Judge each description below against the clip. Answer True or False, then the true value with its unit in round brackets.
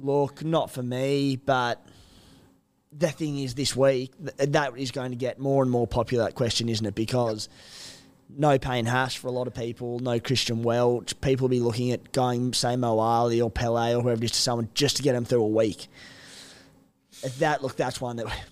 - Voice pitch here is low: True (125 Hz)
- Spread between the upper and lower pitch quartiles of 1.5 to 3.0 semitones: True (2.5 semitones)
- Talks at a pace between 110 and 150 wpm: False (205 wpm)